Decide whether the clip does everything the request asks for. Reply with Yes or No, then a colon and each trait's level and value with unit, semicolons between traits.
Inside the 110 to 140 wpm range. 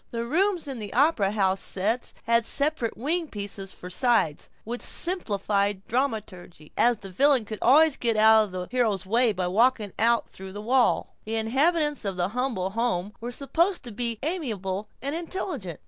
No: average, 175 wpm